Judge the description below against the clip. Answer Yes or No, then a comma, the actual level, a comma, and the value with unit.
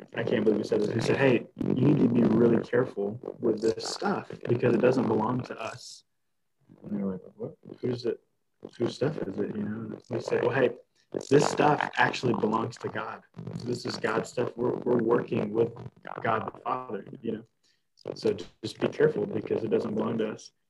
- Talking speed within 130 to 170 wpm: No, average, 200 wpm